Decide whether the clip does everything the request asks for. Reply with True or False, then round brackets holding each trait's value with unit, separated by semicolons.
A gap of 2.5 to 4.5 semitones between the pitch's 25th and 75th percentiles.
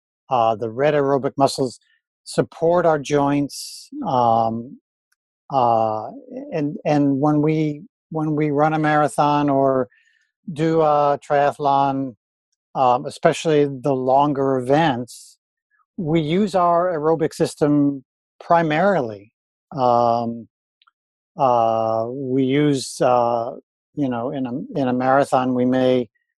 True (3.7 semitones)